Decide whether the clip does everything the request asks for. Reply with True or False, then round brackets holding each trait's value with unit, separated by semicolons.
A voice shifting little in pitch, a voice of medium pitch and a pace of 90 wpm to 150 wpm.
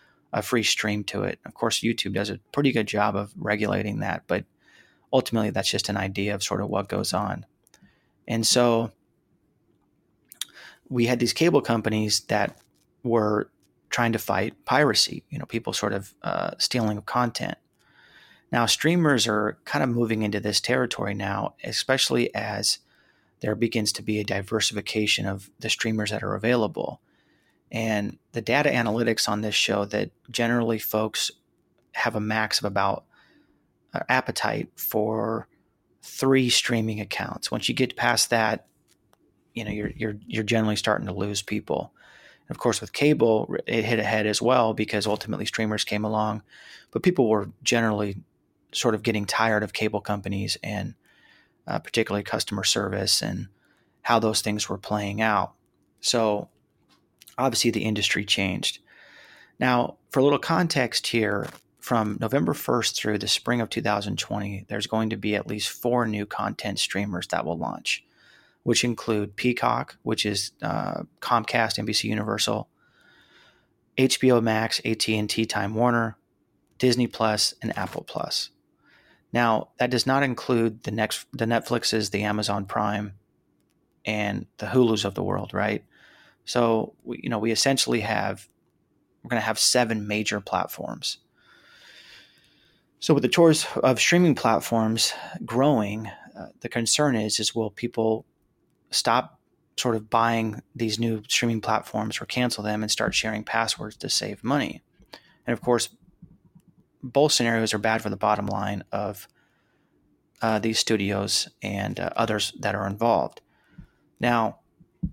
False (2.2 semitones; 110 Hz; 145 wpm)